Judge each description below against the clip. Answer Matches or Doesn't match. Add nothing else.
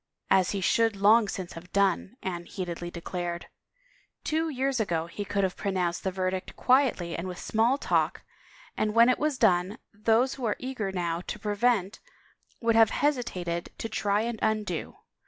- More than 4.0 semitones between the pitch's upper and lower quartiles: Matches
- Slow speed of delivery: Doesn't match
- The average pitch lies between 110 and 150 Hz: Doesn't match